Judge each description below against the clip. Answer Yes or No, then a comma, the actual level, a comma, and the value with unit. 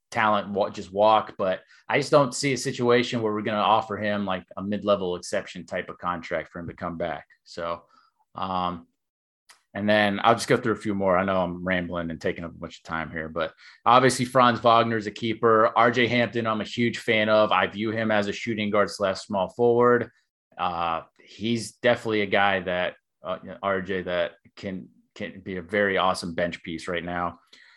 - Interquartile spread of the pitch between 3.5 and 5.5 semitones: Yes, average, 3.8 semitones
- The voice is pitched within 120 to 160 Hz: No, low, 105 Hz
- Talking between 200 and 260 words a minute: Yes, fast, 205 wpm